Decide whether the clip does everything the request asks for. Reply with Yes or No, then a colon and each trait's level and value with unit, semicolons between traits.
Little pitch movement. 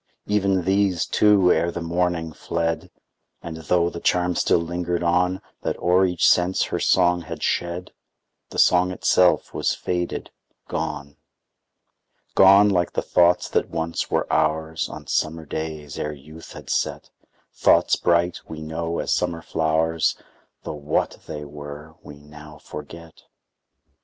Yes: narrow, 2.1 semitones